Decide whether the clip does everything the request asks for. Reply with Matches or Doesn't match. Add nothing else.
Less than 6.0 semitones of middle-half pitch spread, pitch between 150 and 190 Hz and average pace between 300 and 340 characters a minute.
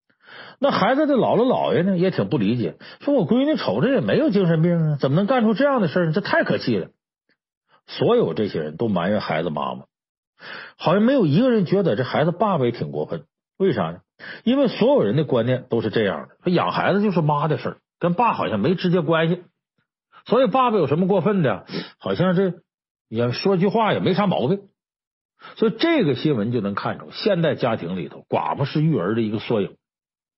Matches